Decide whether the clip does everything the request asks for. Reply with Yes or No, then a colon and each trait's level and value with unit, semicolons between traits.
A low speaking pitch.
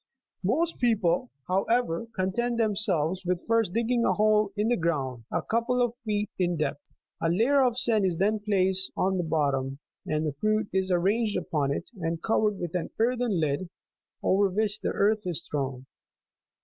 No: high, 195 Hz